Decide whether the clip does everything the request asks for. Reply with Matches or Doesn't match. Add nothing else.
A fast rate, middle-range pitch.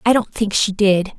Doesn't match